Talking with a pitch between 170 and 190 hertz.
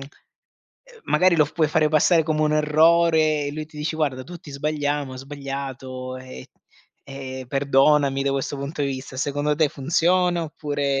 No: medium, 145 Hz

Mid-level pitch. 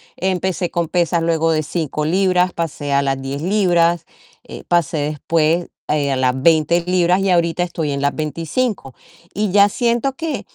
Yes: medium, 170 Hz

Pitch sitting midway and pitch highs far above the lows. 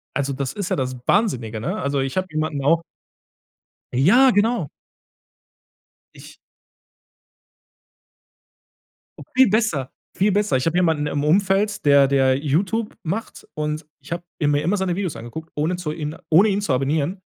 Yes: medium, 155 Hz; wide, 5.7 semitones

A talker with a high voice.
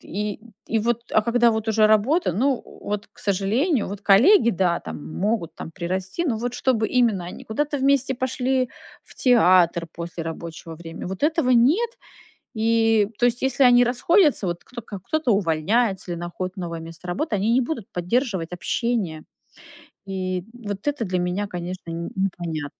Yes: high, 210 Hz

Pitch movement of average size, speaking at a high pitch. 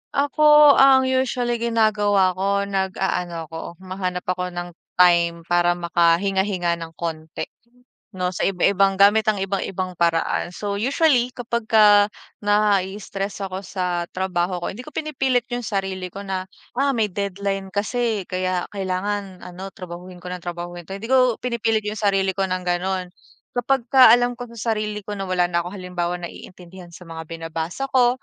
Yes: average, 3.4 semitones; high, 195 Hz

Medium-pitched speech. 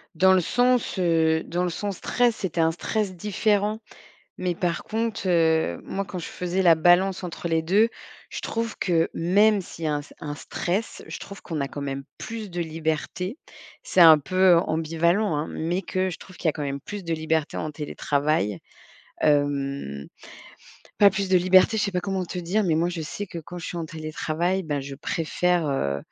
Yes: medium, 175 Hz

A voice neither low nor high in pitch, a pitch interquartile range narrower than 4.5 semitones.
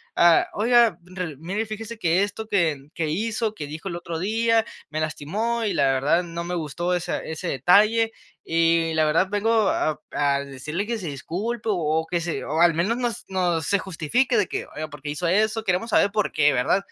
No: medium, 175 Hz; average, 5.3 semitones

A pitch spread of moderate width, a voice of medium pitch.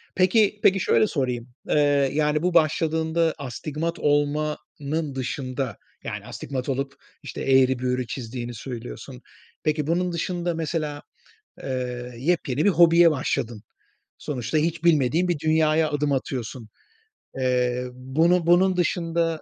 Yes: average, 4.4 semitones; medium, 145 Hz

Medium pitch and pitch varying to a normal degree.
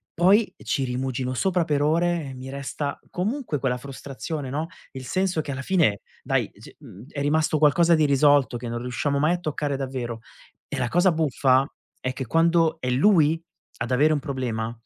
Yes: medium, 145 Hz; average, 4.0 semitones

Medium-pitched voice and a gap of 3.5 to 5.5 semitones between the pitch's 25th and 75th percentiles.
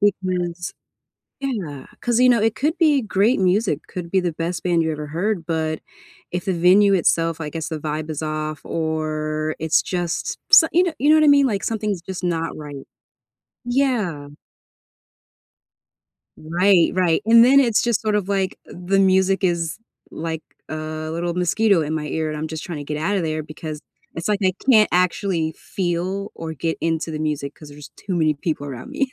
Yes: medium, 175 Hz; average, 4.3 semitones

